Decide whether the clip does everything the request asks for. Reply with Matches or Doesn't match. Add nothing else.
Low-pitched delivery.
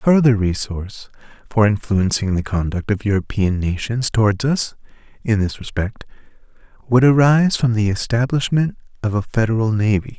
Matches